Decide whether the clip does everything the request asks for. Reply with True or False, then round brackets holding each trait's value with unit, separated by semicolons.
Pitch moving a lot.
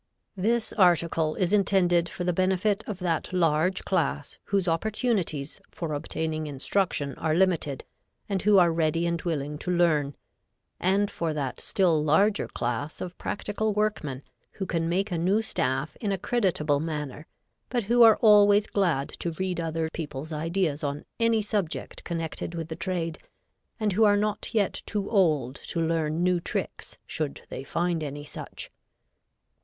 False (4.2 semitones)